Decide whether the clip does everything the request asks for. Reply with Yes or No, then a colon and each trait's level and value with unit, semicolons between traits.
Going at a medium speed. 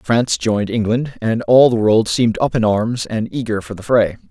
No: fast, 225 wpm